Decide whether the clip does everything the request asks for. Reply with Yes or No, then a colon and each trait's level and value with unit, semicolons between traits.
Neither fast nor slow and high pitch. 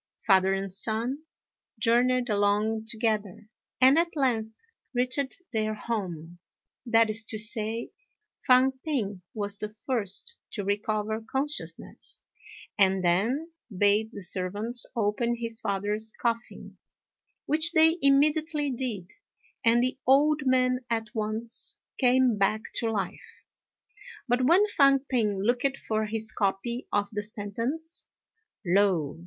No: slow, 120 wpm; high, 225 Hz